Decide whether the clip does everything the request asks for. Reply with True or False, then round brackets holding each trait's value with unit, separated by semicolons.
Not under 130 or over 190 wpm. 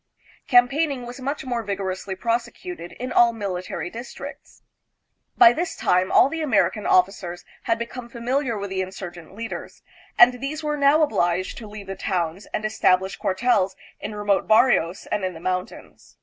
True (165 wpm)